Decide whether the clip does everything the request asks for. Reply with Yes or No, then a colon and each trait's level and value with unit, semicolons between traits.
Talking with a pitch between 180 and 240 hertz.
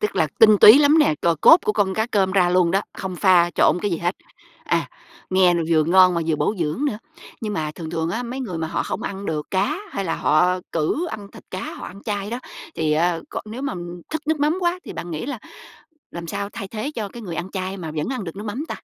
Yes: high, 190 Hz